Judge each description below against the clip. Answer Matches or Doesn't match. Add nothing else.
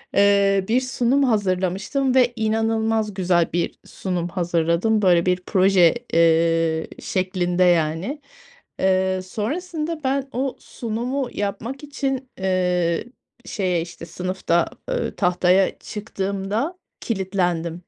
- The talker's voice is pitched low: Doesn't match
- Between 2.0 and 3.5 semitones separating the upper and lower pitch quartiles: Doesn't match